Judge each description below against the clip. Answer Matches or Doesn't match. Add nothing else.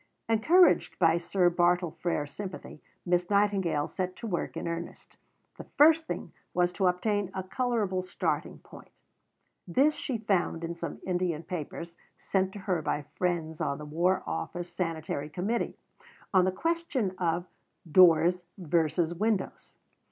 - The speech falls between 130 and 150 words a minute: Matches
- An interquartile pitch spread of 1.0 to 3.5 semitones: Matches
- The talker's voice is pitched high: Doesn't match